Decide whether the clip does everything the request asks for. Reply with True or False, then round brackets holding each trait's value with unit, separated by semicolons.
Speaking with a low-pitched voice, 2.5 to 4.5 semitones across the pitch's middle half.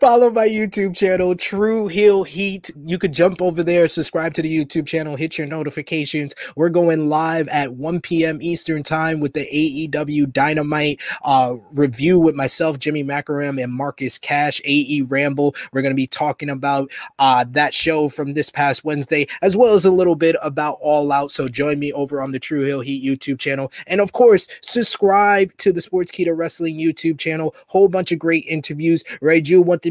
False (155 Hz; 3.3 semitones)